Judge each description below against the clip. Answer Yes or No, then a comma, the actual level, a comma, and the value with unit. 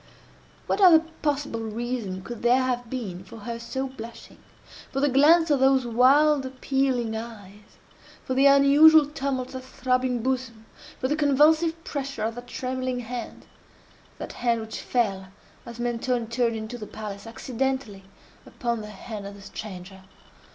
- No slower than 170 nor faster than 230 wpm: No, average, 145 wpm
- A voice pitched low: No, high, 245 Hz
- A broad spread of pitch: No, average, 3.2 semitones